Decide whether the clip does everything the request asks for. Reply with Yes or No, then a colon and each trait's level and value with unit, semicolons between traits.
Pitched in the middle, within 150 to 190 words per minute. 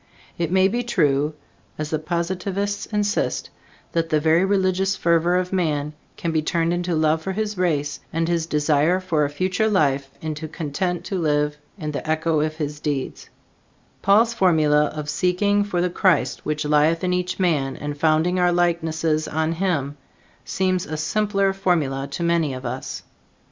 Yes: medium, 165 Hz; average, 170 wpm